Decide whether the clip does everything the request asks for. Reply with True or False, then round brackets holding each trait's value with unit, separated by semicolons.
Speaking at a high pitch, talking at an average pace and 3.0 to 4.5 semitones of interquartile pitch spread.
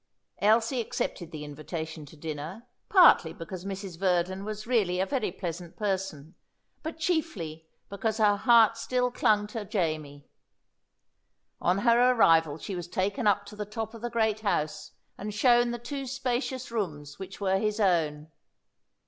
False (200 Hz; 155 wpm; 5.6 semitones)